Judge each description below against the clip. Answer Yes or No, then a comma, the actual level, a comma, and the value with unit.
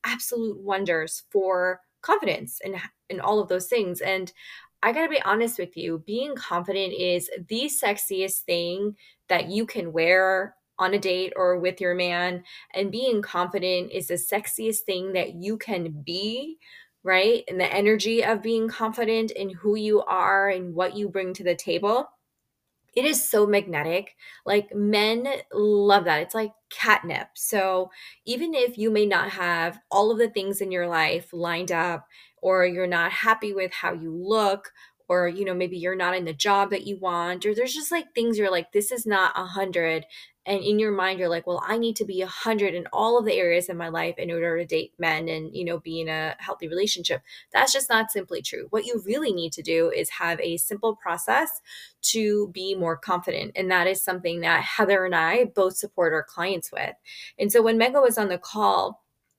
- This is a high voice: Yes, high, 195 Hz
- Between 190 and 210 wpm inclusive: Yes, average, 200 wpm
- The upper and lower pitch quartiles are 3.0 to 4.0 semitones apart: Yes, average, 3.5 semitones